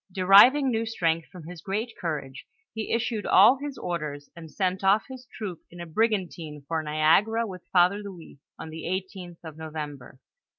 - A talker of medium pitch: Yes, medium, 180 Hz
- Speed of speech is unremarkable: Yes, average, 170 wpm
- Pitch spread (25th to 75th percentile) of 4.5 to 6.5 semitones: Yes, average, 4.9 semitones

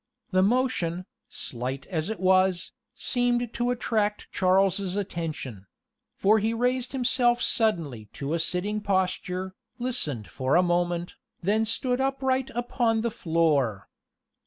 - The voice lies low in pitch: No, high, 195 Hz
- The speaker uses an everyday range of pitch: No, wide, 6.0 semitones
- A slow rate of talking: Yes, slow, 130 wpm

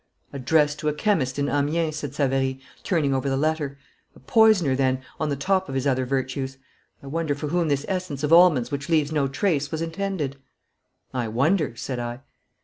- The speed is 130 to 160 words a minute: No, average, 195 wpm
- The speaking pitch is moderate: Yes, medium, 145 Hz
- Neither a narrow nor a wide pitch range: Yes, average, 3.3 semitones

